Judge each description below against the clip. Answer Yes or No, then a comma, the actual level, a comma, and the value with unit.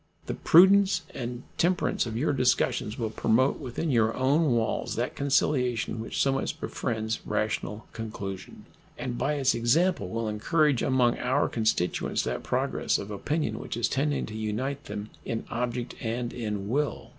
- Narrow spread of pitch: No, average, 4.0 semitones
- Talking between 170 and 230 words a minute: No, average, 155 wpm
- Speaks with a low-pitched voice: Yes, low, 120 Hz